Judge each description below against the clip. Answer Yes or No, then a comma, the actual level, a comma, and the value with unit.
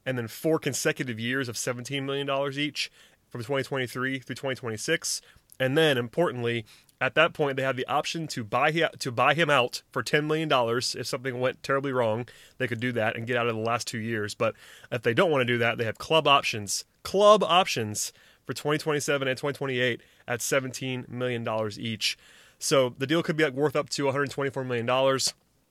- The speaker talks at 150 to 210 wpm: Yes, average, 195 wpm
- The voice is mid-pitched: No, low, 130 Hz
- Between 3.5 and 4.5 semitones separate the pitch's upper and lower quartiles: No, average, 3.1 semitones